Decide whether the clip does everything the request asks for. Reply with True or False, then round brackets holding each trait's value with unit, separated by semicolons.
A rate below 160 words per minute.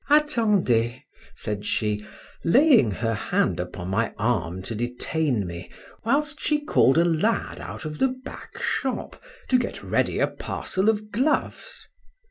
True (140 wpm)